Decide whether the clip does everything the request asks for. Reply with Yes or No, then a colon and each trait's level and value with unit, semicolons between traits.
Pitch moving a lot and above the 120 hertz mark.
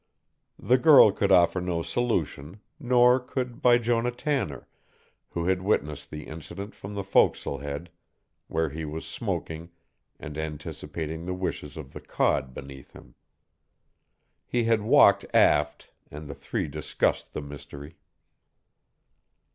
No: wide, 7.4 semitones; very low, 85 Hz